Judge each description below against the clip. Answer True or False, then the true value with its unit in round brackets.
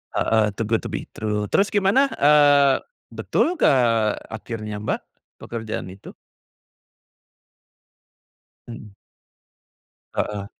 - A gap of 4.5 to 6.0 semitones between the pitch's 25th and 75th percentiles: True (5.2 semitones)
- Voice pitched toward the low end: True (115 Hz)